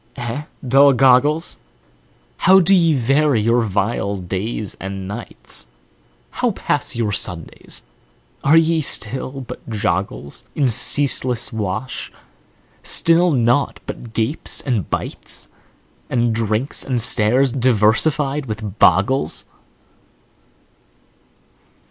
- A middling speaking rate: No, slow, 100 wpm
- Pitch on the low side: Yes, low, 120 Hz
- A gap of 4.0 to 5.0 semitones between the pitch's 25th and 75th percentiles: Yes, average, 4.5 semitones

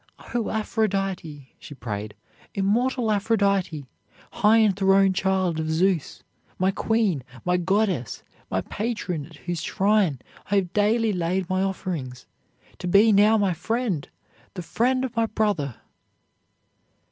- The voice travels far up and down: No, average, 4.2 semitones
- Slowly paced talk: Yes, slow, 125 wpm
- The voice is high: Yes, high, 195 Hz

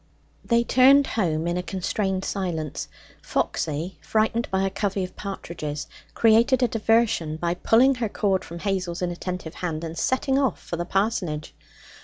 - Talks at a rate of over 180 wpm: No, average, 155 wpm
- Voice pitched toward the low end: No, high, 190 Hz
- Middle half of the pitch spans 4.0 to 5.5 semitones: Yes, average, 4.8 semitones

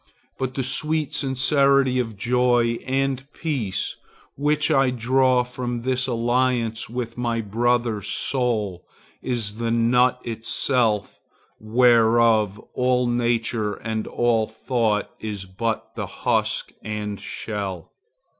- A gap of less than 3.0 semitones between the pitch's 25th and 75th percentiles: Yes, narrow, 2.5 semitones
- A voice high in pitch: No, low, 120 Hz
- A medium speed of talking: No, slow, 110 wpm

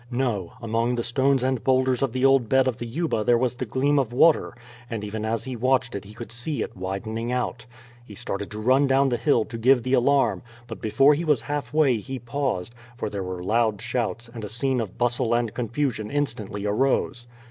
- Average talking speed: No, fast, 215 wpm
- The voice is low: Yes, low, 120 Hz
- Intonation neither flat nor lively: Yes, average, 3.2 semitones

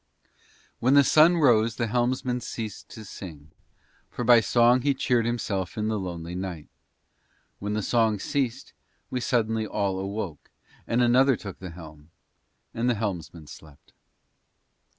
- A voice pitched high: No, low, 110 Hz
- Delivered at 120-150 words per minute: Yes, average, 145 wpm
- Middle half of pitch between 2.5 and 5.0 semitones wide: Yes, average, 4.5 semitones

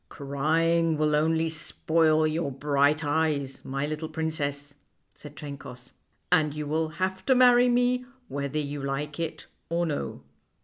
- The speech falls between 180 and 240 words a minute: No, average, 150 wpm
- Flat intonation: Yes, narrow, 2.3 semitones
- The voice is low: No, medium, 155 Hz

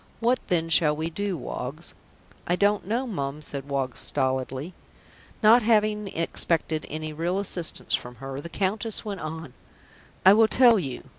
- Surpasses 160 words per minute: No, average, 155 wpm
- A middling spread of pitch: No, wide, 6.3 semitones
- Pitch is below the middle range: No, medium, 170 Hz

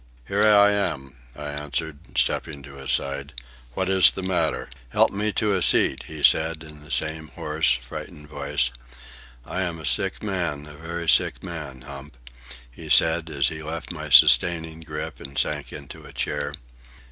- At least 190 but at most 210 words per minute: No, average, 170 wpm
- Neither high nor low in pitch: No, very low, 80 Hz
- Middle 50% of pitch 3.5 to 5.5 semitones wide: No, average, 2.9 semitones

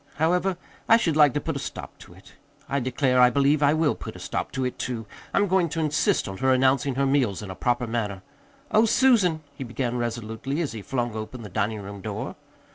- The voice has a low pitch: Yes, low, 130 Hz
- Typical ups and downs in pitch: Yes, average, 4.9 semitones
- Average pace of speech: No, fast, 225 wpm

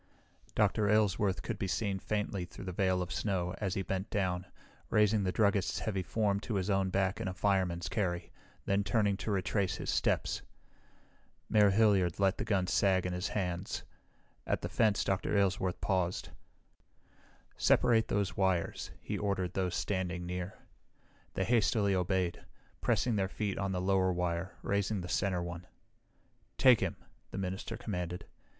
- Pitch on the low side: Yes, very low, 95 Hz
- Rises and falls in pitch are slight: Yes, narrow, 2.0 semitones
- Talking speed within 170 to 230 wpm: No, average, 160 wpm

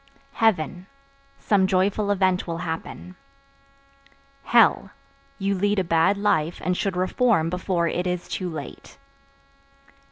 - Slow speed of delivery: Yes, slow, 120 wpm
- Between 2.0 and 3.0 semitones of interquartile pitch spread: Yes, narrow, 2.6 semitones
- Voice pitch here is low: No, medium, 185 Hz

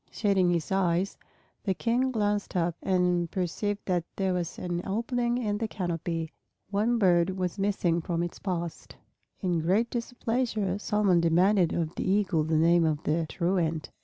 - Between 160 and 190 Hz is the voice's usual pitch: Yes, medium, 185 Hz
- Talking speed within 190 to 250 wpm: No, average, 160 wpm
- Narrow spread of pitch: No, average, 3.4 semitones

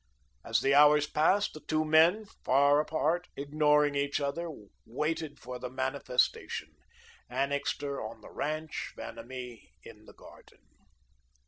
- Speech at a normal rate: No, slow, 125 wpm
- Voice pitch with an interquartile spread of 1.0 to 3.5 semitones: Yes, average, 2.8 semitones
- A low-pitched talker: No, medium, 145 Hz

